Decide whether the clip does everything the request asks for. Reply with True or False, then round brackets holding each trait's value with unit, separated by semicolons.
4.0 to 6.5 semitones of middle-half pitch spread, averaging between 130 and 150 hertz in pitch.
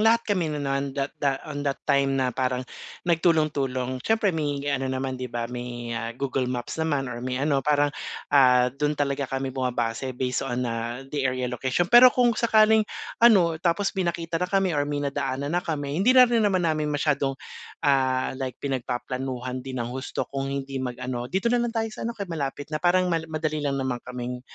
True (4.4 semitones; 140 Hz)